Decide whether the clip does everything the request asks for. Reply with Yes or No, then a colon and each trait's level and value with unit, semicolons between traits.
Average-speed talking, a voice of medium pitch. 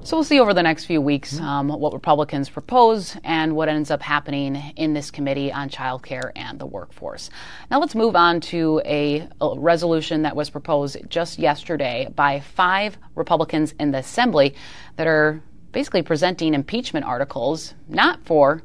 Yes: average, 170 wpm; medium, 155 Hz